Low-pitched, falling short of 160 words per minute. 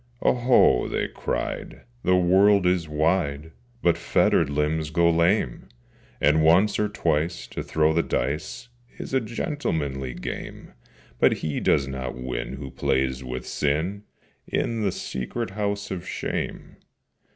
Yes: very low, 80 Hz; slow, 135 wpm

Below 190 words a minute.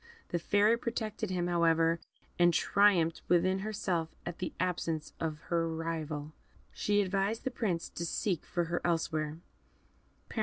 Yes: average, 140 wpm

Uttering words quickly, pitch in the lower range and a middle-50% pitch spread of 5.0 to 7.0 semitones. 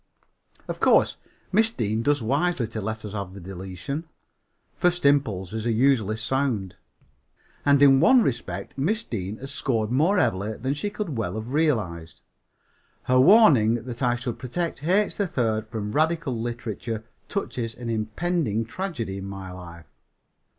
No: average, 150 wpm; low, 120 Hz; average, 5.3 semitones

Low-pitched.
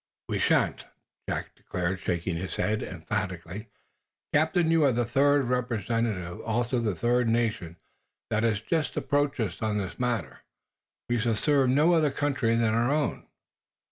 Yes: low, 115 Hz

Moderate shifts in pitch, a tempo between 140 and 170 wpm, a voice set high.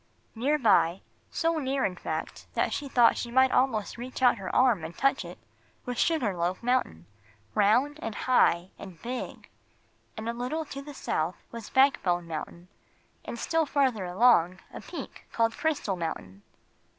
No: wide, 6.4 semitones; average, 165 wpm; high, 235 Hz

